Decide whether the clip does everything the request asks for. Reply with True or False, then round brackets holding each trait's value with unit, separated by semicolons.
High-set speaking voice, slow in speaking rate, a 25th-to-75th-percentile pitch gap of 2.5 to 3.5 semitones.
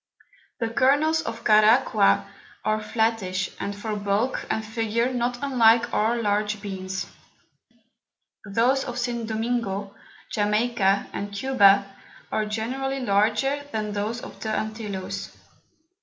True (220 Hz; 115 wpm; 2.8 semitones)